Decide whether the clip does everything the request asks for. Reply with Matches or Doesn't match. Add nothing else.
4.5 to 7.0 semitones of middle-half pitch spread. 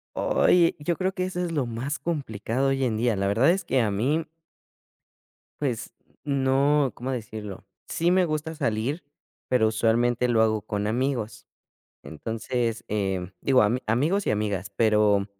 Matches